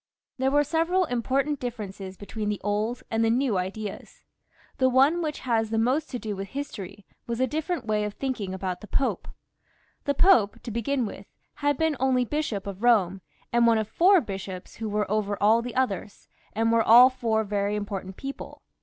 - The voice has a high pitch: Yes, high, 225 Hz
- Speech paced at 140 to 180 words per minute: No, average, 190 wpm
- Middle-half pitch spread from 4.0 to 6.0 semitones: Yes, average, 4.4 semitones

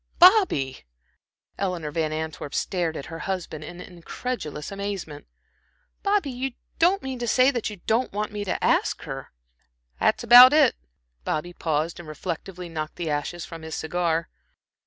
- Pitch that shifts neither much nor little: No, wide, 7.3 semitones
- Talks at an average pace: Yes, average, 155 wpm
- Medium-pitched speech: Yes, medium, 175 Hz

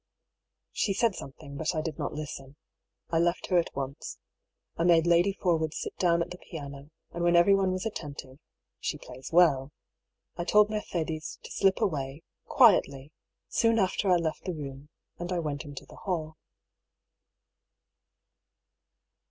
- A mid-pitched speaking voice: Yes, medium, 165 Hz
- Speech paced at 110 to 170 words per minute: Yes, average, 150 wpm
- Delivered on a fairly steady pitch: No, average, 4.0 semitones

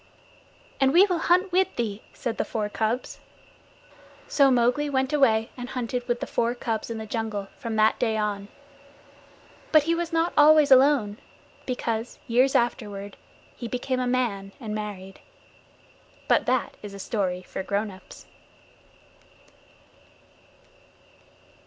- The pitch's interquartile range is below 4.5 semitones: Yes, average, 4.1 semitones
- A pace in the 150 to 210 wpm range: No, average, 140 wpm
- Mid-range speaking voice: No, high, 235 Hz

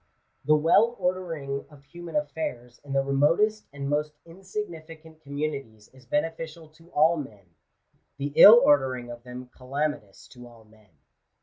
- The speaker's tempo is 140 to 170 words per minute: Yes, average, 150 wpm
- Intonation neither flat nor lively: Yes, average, 4.2 semitones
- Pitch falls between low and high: Yes, medium, 145 Hz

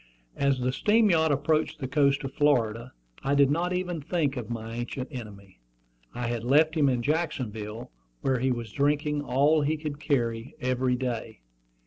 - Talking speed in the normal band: Yes, average, 170 wpm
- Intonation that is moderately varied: Yes, average, 3.9 semitones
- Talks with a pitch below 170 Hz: Yes, low, 135 Hz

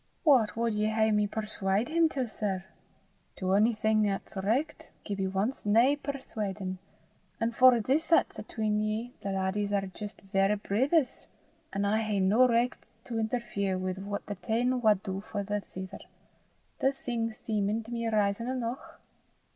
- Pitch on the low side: No, high, 215 Hz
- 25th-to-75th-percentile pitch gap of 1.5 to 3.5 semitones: Yes, average, 3.0 semitones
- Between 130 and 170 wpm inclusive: Yes, average, 155 wpm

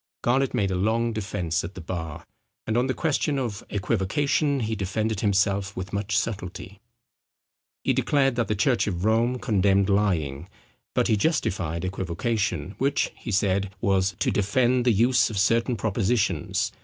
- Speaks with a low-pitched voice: Yes, low, 100 Hz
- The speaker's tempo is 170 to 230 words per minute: No, average, 155 wpm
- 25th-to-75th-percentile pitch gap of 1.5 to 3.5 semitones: No, average, 4.0 semitones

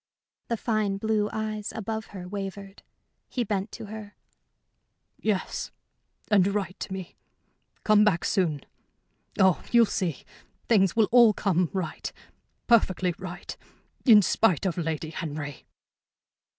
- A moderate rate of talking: No, slow, 125 wpm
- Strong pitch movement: No, average, 2.9 semitones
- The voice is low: No, high, 200 Hz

